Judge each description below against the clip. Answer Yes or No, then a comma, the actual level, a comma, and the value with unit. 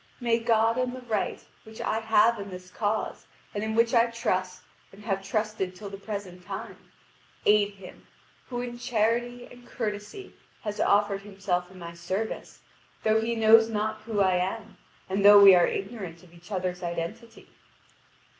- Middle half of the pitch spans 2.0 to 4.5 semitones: Yes, average, 3.1 semitones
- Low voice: No, high, 210 Hz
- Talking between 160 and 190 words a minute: Yes, average, 170 wpm